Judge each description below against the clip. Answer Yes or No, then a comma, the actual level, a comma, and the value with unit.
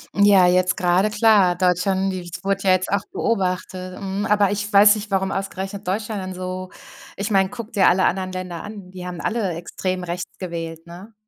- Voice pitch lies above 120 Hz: Yes, high, 190 Hz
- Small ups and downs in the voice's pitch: Yes, narrow, 1.9 semitones